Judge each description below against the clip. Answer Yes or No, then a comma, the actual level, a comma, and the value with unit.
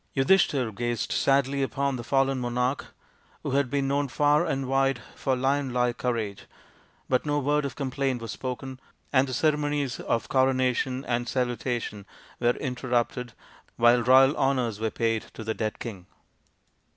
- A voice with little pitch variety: Yes, narrow, 2.2 semitones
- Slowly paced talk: No, average, 155 wpm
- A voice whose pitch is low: Yes, low, 130 Hz